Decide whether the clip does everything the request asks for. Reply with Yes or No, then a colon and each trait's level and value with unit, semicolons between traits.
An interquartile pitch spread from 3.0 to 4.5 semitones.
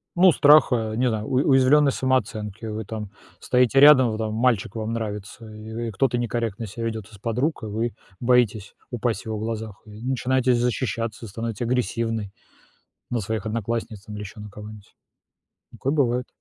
No: narrow, 2.5 semitones